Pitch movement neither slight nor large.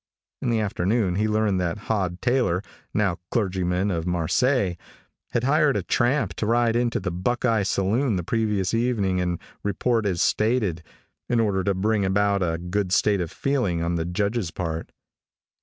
Yes: average, 4.4 semitones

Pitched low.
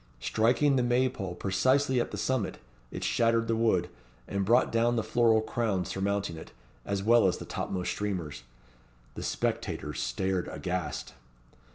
Yes: low, 105 Hz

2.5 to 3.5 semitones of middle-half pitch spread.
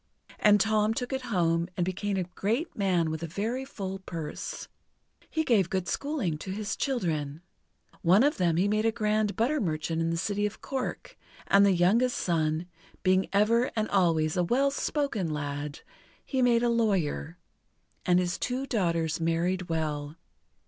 No: average, 5.3 semitones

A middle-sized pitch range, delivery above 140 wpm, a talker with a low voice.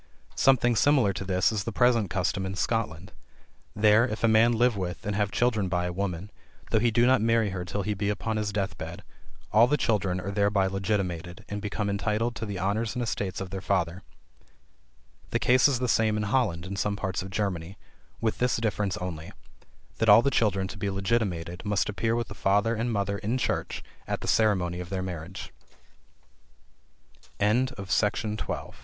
Yes: average, 3.0 semitones; average, 190 wpm; low, 105 Hz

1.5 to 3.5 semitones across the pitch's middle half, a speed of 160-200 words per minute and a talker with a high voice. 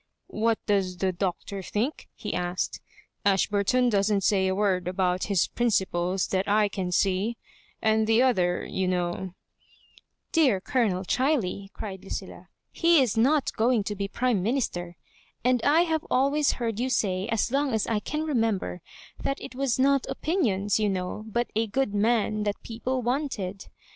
No: average, 4.8 semitones; average, 180 wpm; high, 210 Hz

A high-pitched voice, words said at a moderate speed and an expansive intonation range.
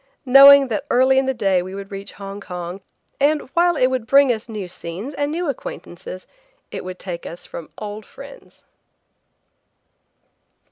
Yes: high, 220 Hz; average, 160 wpm; wide, 6.6 semitones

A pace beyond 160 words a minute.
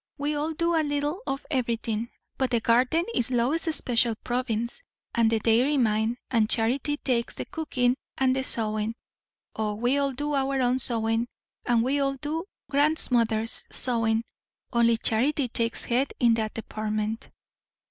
No: average, 155 wpm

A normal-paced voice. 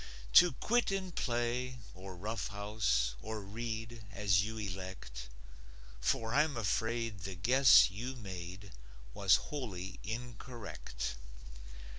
No: slow, 105 wpm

